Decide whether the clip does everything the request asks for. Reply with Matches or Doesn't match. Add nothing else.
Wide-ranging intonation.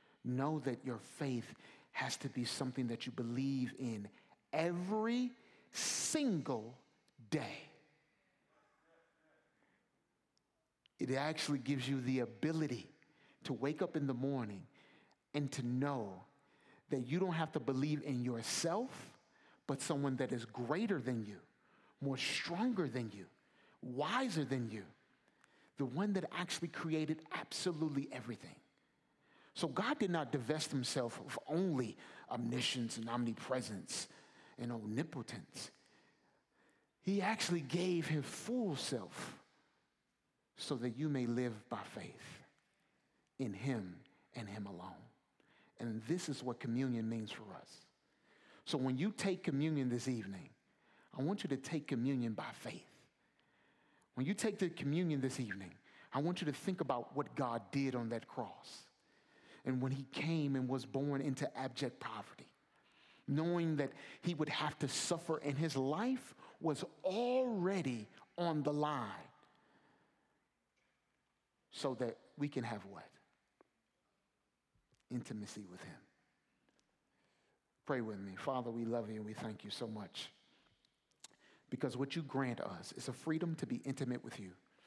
Doesn't match